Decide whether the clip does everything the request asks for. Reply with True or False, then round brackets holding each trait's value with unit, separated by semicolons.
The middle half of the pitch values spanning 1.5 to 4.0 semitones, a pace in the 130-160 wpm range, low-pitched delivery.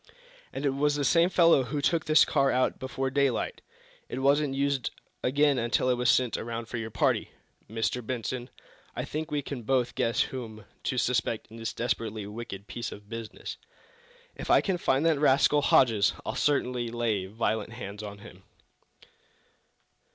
False (3.7 semitones; 170 wpm; 125 Hz)